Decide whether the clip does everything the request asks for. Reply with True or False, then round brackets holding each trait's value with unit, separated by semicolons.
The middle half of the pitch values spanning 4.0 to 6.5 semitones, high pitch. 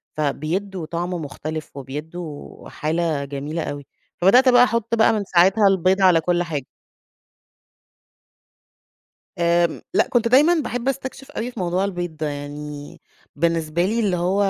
False (4.7 semitones; 175 Hz)